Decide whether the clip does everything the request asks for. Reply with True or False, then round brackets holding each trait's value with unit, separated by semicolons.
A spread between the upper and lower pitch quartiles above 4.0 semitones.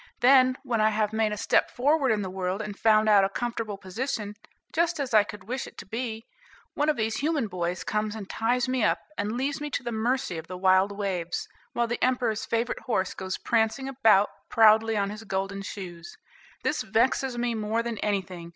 False (3.6 semitones)